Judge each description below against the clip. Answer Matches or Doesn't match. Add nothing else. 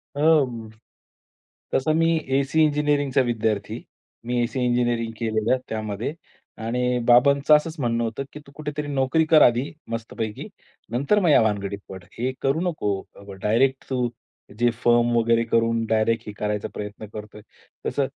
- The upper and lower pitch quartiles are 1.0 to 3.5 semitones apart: Doesn't match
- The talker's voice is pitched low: Matches